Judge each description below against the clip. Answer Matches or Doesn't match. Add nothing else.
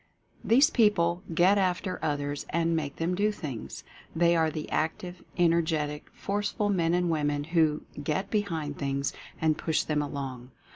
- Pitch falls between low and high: Matches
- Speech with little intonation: Doesn't match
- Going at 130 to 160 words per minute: Matches